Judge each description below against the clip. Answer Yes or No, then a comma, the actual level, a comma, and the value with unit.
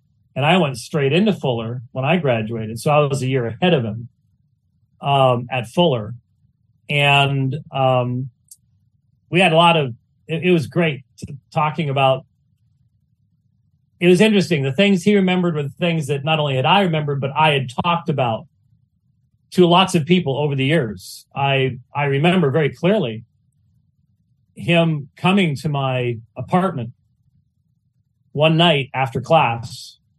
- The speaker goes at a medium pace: Yes, average, 150 wpm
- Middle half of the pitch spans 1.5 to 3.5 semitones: No, average, 4.4 semitones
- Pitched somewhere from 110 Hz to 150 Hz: Yes, medium, 140 Hz